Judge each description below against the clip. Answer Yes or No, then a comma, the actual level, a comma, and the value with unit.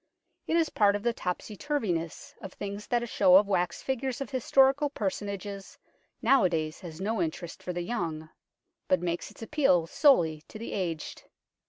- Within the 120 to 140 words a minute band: No, average, 170 wpm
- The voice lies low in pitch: No, high, 200 Hz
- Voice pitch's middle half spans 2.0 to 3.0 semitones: No, wide, 5.6 semitones